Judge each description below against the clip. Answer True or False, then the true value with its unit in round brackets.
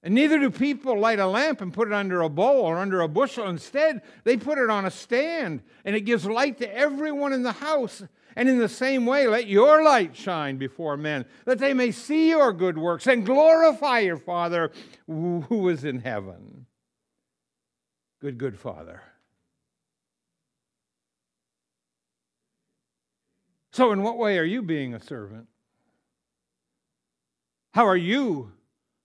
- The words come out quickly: False (155 wpm)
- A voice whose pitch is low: False (200 Hz)